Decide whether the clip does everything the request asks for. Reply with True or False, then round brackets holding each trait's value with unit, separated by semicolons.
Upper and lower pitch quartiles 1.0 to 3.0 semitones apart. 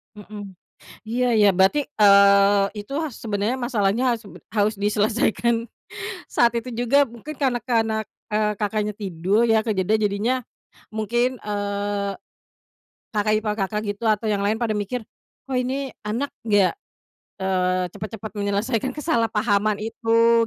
True (2.4 semitones)